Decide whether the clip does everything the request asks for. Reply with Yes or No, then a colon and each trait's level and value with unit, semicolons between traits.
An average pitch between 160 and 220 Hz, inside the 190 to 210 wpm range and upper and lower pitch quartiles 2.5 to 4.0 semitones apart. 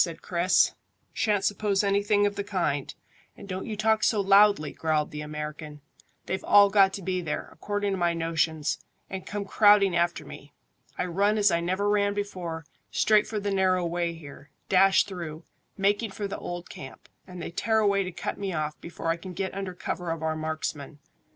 Yes: medium, 185 Hz; average, 195 wpm; average, 3.6 semitones